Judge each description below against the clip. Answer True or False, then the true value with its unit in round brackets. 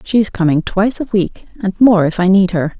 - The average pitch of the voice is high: True (200 Hz)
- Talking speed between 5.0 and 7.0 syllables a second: True (5.2 syllables/s)